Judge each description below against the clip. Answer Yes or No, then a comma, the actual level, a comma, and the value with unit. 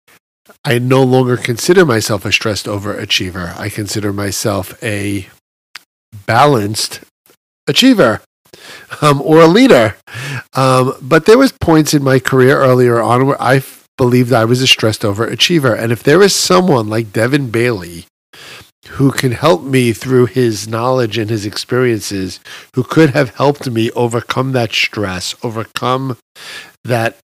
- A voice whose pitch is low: Yes, low, 125 Hz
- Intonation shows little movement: No, average, 3.7 semitones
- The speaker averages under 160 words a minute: Yes, average, 145 wpm